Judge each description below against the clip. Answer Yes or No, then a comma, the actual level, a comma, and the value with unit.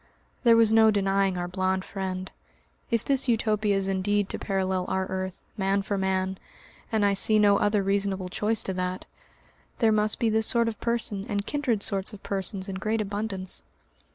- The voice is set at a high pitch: Yes, high, 200 Hz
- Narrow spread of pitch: Yes, narrow, 2.3 semitones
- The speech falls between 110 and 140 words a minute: No, average, 180 wpm